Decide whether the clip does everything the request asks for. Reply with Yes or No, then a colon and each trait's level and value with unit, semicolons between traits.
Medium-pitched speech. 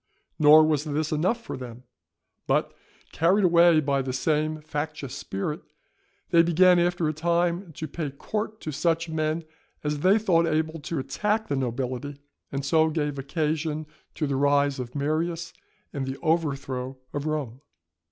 Yes: medium, 155 Hz